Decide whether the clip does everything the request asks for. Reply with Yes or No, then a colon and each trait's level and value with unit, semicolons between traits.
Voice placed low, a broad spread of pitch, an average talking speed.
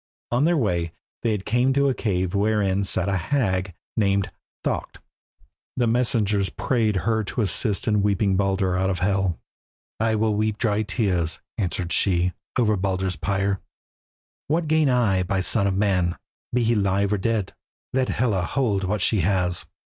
No: low, 100 Hz; average, 3.3 semitones; average, 165 wpm